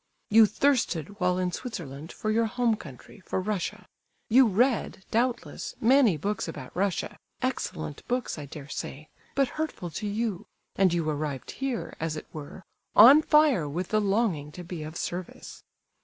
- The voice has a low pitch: No, high, 195 Hz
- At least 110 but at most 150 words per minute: No, average, 160 wpm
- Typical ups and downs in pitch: No, wide, 6.4 semitones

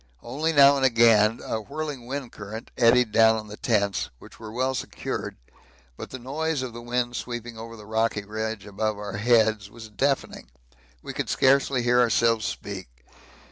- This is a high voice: No, low, 115 Hz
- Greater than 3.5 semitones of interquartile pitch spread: No, average, 2.9 semitones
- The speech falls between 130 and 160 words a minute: No, average, 175 wpm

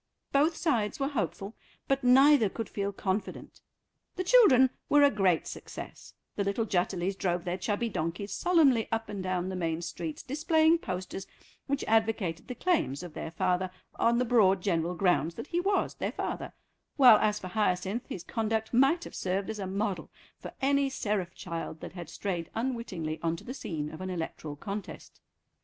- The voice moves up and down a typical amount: No, wide, 5.9 semitones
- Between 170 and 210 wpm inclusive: Yes, average, 180 wpm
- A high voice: Yes, high, 200 Hz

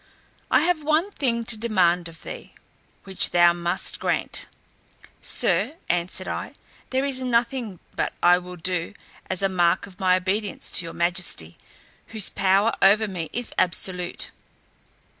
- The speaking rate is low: No, average, 145 wpm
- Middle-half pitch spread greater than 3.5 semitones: Yes, average, 4.7 semitones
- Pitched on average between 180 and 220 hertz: Yes, high, 190 Hz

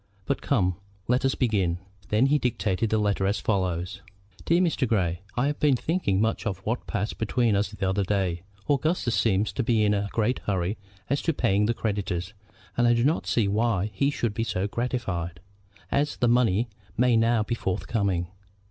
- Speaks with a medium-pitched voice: No, low, 110 Hz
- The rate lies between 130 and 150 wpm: No, average, 190 wpm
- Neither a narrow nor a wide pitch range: Yes, average, 4.0 semitones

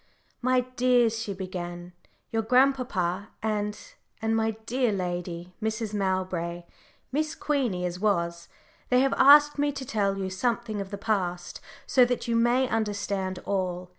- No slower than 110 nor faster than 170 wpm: Yes, average, 150 wpm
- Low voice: No, high, 210 Hz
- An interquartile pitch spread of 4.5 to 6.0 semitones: Yes, average, 4.9 semitones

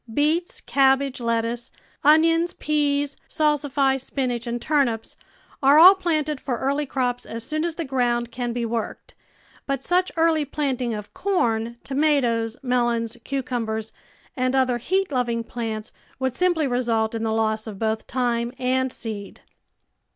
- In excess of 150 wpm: No, average, 145 wpm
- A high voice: Yes, very high, 255 Hz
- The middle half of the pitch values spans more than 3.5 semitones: Yes, average, 3.9 semitones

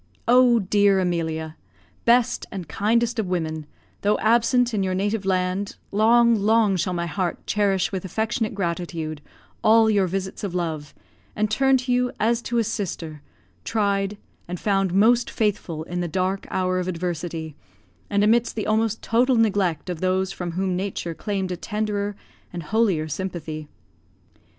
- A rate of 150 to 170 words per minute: Yes, average, 155 wpm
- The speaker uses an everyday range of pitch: Yes, average, 3.7 semitones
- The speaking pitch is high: Yes, high, 195 Hz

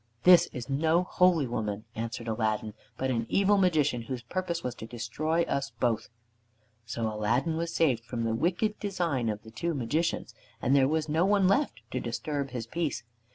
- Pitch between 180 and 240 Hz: No, low, 135 Hz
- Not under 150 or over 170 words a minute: No, average, 180 wpm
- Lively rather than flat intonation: Yes, wide, 6.6 semitones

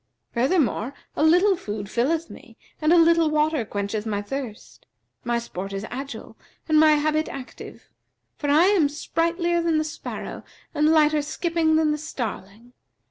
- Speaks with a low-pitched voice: No, very high, 300 Hz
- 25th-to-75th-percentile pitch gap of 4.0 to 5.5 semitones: Yes, average, 5.2 semitones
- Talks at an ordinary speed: Yes, average, 160 wpm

